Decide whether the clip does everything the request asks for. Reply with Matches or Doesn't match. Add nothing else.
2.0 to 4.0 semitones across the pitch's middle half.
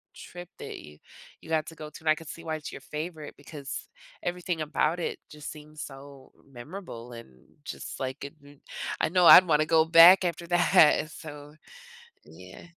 Matches